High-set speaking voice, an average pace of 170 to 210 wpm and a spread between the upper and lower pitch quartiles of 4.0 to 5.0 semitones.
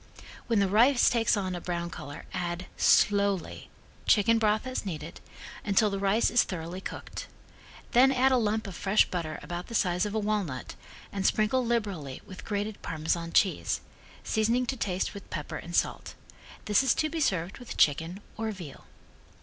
Yes: high, 200 Hz; average, 175 wpm; average, 4.3 semitones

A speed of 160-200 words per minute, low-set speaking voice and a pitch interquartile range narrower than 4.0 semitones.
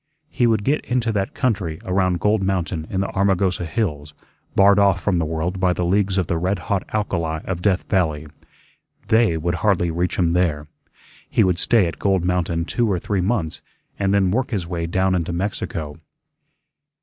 Yes: average, 185 wpm; very low, 95 Hz; average, 2.9 semitones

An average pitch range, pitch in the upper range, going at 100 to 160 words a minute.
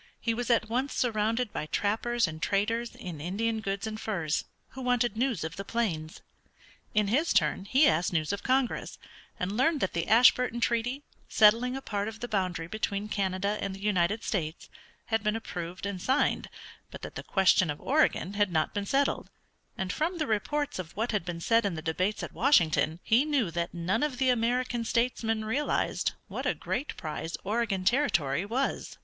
No: average, 4.6 semitones; high, 215 Hz; average, 190 wpm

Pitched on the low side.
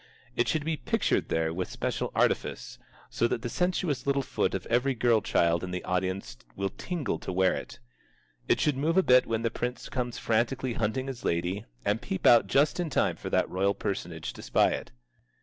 Yes: low, 115 Hz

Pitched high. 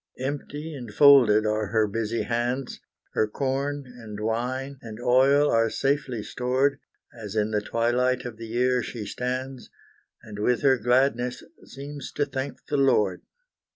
No: low, 125 Hz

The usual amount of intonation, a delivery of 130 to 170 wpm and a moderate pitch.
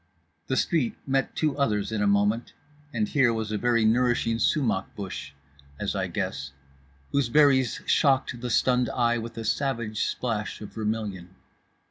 No: average, 3.7 semitones; average, 155 wpm; low, 115 Hz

